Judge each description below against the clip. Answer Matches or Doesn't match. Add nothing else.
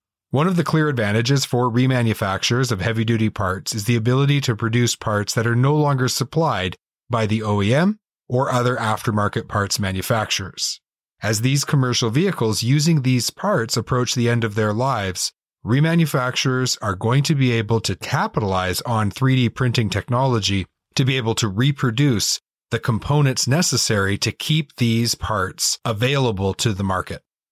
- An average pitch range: Matches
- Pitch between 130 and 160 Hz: Doesn't match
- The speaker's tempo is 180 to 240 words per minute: Doesn't match